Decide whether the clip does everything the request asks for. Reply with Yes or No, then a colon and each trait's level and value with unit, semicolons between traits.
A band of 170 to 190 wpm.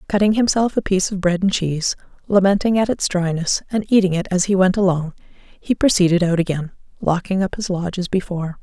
No: average, 200 wpm